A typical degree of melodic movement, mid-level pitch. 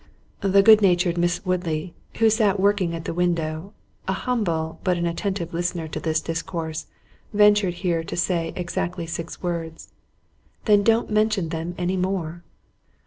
Yes: average, 3.0 semitones; medium, 175 Hz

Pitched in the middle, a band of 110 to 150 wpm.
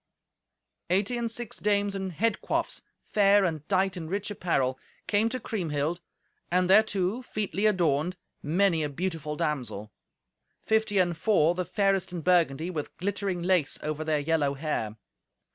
Yes: medium, 180 Hz; average, 145 wpm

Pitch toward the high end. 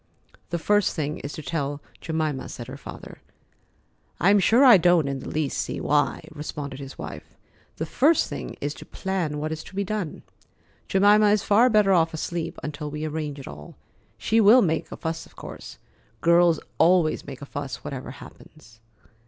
No: medium, 160 Hz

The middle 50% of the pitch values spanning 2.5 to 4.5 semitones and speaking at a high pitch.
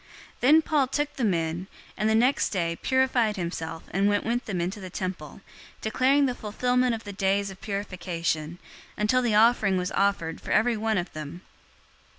No: average, 5.1 semitones; high, 205 Hz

